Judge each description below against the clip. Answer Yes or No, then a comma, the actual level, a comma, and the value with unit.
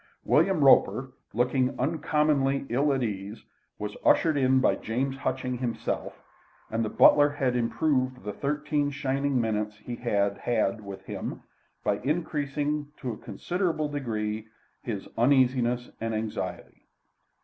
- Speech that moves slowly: Yes, slow, 130 wpm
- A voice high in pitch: No, low, 130 Hz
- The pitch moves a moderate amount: Yes, average, 4.1 semitones